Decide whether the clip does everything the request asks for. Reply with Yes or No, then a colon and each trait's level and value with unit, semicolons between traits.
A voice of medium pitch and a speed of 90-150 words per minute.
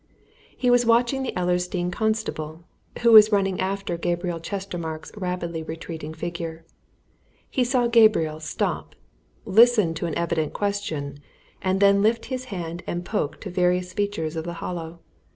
Yes: medium, 180 Hz; average, 145 wpm